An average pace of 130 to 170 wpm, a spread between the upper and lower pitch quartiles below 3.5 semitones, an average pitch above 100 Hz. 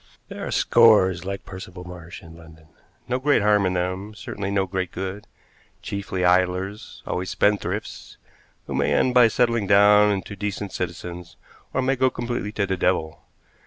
No: average, 160 wpm; narrow, 2.5 semitones; very low, 95 Hz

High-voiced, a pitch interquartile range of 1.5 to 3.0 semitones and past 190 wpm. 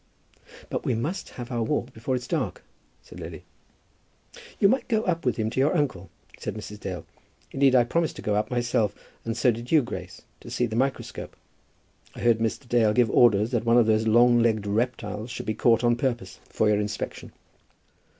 No: low, 120 Hz; narrow, 2.6 semitones; average, 200 wpm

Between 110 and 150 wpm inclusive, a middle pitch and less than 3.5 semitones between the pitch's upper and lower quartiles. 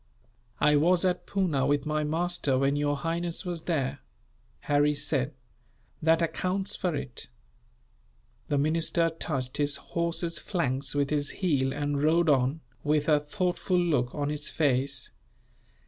Yes: average, 140 wpm; medium, 150 Hz; average, 3.0 semitones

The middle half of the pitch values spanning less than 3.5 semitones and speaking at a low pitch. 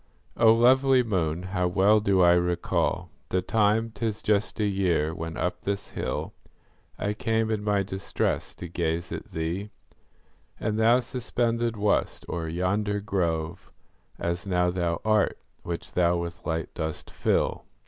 No: average, 3.9 semitones; very low, 95 Hz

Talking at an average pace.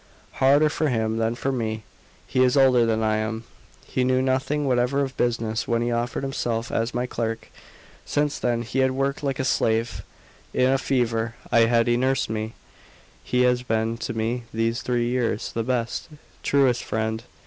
Yes: average, 180 wpm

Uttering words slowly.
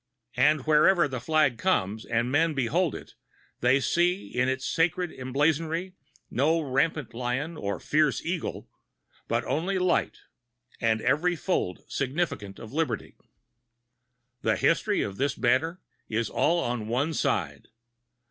Yes: slow, 130 wpm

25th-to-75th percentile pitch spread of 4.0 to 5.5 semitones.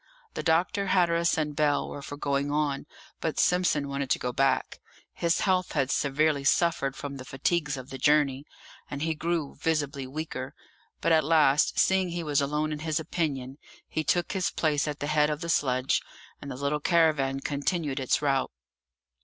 No: average, 2.7 semitones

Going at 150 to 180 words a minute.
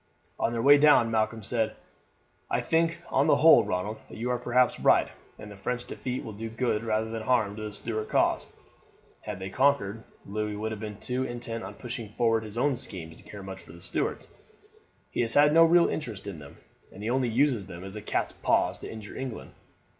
No: fast, 205 wpm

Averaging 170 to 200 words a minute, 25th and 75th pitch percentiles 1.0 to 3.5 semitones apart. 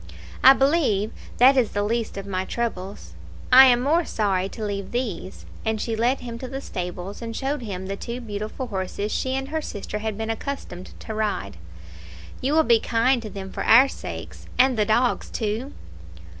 No: average, 190 wpm; average, 4.1 semitones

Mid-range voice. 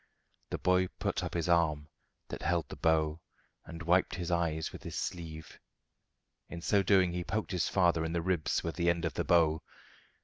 No: very low, 85 Hz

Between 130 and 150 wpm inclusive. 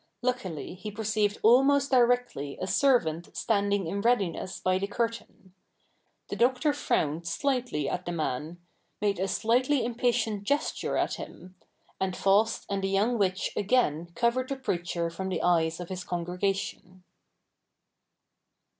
Yes: slow, 135 wpm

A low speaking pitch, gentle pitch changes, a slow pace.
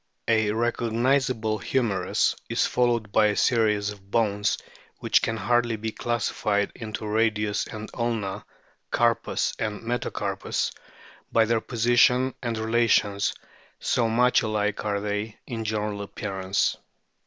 Yes: low, 110 Hz; narrow, 2.2 semitones; slow, 125 wpm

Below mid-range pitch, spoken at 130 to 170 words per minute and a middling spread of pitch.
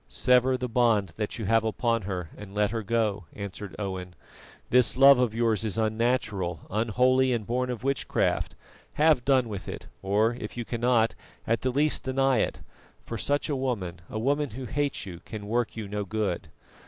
No: low, 115 Hz; average, 185 wpm; average, 3.6 semitones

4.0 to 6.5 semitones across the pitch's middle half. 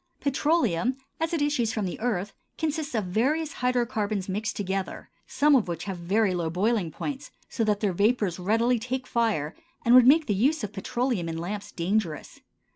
Yes: average, 5.0 semitones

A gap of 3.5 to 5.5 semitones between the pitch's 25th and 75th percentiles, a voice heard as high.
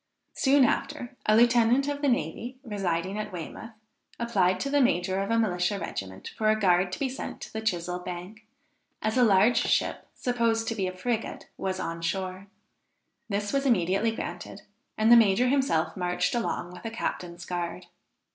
Yes: average, 4.7 semitones; high, 210 Hz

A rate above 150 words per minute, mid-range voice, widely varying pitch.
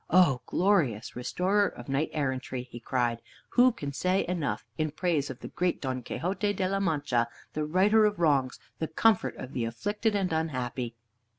Yes: average, 175 wpm; medium, 155 Hz; wide, 6.6 semitones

